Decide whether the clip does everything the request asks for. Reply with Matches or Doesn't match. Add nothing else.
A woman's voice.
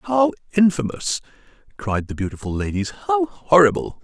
Doesn't match